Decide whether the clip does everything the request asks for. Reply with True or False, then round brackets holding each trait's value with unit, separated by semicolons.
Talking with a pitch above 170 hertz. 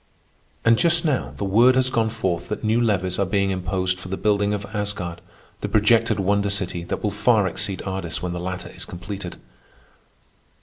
False (100 Hz)